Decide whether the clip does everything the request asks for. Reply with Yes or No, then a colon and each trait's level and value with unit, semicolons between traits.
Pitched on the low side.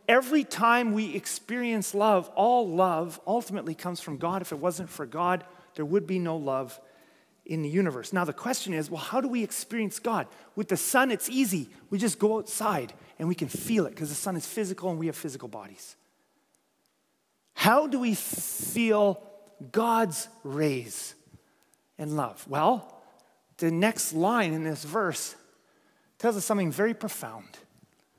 No: high, 190 Hz